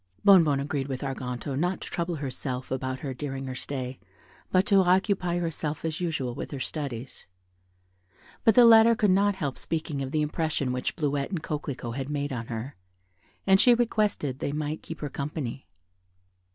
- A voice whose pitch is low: No, medium, 145 Hz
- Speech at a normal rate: Yes, average, 175 wpm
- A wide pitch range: No, average, 4.9 semitones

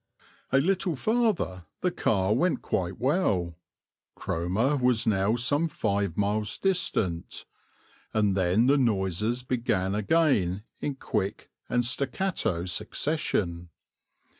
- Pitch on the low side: Yes, low, 110 Hz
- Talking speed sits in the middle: No, slow, 110 wpm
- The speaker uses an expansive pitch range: Yes, wide, 6.9 semitones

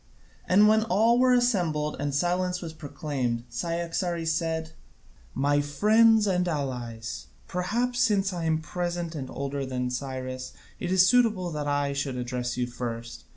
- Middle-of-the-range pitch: Yes, medium, 160 Hz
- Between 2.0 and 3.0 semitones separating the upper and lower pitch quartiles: No, wide, 5.6 semitones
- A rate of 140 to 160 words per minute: Yes, average, 150 wpm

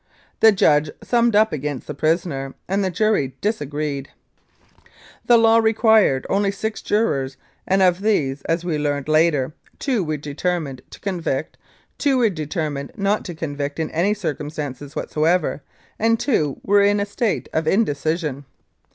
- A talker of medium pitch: Yes, medium, 165 Hz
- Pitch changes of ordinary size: No, wide, 5.9 semitones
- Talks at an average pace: Yes, average, 150 wpm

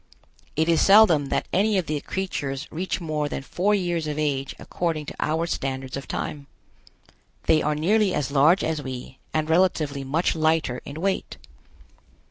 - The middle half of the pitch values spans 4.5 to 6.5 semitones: No, average, 3.7 semitones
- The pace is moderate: Yes, average, 165 wpm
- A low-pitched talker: No, medium, 155 Hz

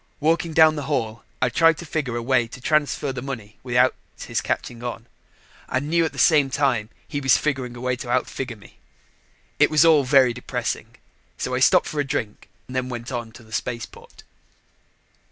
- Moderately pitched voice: No, low, 130 Hz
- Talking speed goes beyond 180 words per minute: Yes, average, 190 wpm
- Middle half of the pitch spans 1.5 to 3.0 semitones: No, average, 3.4 semitones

